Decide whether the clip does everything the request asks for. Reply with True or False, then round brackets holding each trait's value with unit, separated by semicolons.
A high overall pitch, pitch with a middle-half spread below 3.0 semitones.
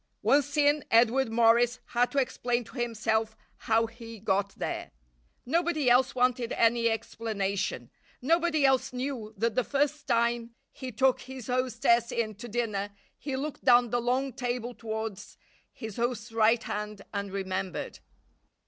True (240 Hz; 2.6 semitones)